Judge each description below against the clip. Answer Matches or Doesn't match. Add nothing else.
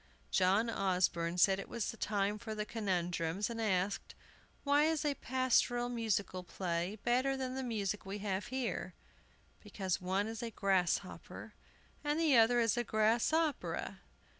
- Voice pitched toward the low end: Doesn't match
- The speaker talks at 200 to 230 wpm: Doesn't match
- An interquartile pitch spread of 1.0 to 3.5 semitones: Doesn't match